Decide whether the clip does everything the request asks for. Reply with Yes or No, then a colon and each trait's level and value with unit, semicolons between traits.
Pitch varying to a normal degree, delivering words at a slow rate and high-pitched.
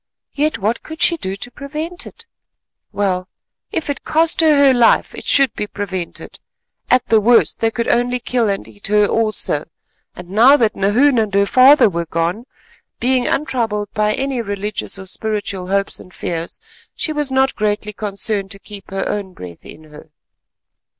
No: average, 4.9 semitones; average, 175 wpm; high, 215 Hz